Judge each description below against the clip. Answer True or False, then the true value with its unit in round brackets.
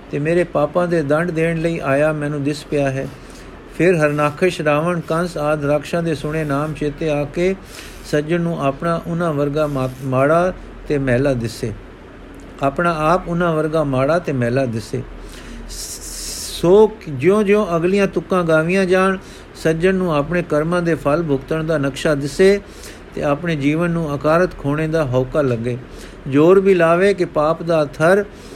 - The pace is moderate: True (155 wpm)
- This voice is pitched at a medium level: True (155 Hz)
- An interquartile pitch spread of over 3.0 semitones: True (3.4 semitones)